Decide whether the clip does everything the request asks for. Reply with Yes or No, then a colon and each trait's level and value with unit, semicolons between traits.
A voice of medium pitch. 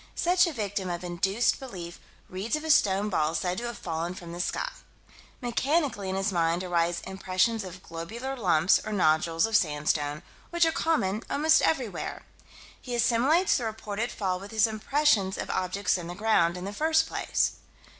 No: high, 200 Hz